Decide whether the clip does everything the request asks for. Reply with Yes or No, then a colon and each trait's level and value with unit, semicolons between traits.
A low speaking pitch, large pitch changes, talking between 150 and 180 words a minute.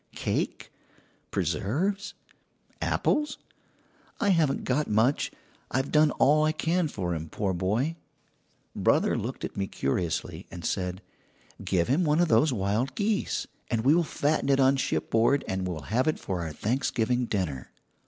Yes: low, 125 Hz; wide, 8.1 semitones; average, 155 wpm